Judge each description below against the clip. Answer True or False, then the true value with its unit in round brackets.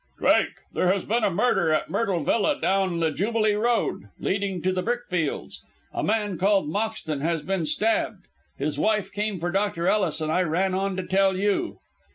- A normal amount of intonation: True (3.6 semitones)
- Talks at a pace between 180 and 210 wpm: True (185 wpm)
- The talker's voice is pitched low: False (195 Hz)